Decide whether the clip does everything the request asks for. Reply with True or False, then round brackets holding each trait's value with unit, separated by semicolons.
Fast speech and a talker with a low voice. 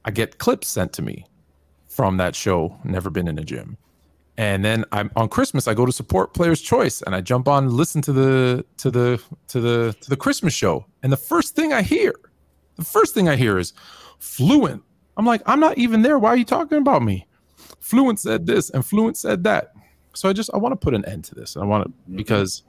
True (235 wpm; 130 Hz)